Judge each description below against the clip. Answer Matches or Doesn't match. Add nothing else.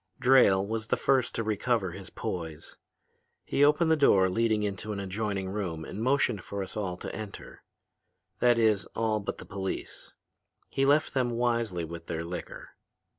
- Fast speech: Doesn't match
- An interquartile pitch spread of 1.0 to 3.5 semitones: Doesn't match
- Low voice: Matches